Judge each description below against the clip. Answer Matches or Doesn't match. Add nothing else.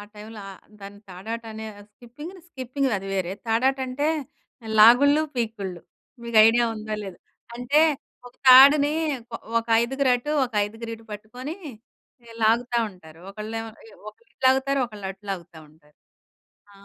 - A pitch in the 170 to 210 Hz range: Doesn't match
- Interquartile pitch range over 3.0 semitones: Matches